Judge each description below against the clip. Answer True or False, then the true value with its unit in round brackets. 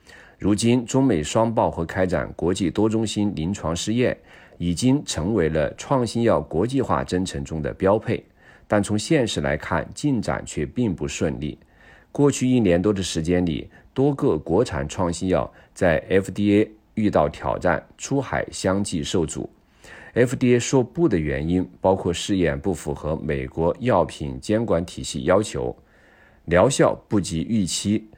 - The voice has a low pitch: True (95 Hz)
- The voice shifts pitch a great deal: True (5.8 semitones)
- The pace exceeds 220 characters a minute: True (230 characters per minute)